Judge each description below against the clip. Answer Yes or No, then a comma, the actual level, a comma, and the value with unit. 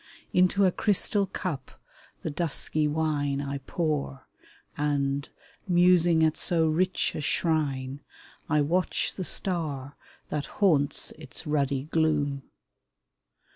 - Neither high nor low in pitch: Yes, medium, 155 Hz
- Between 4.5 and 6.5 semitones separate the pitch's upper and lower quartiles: No, average, 3.5 semitones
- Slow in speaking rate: Yes, slow, 110 wpm